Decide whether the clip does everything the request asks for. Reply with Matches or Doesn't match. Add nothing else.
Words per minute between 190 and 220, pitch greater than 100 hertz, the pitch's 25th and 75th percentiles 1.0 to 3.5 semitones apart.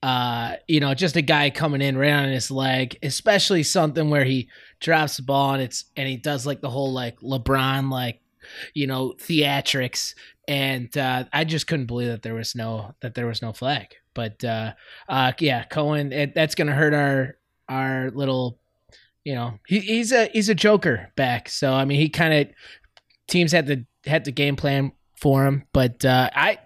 Matches